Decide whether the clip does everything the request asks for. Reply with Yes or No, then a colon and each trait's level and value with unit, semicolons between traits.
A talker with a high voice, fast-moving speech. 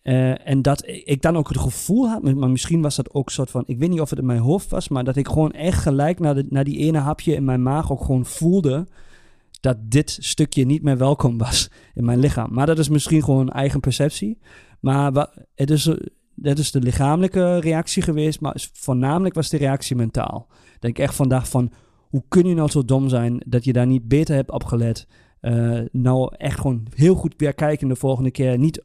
No: medium, 140 Hz; fast, 225 wpm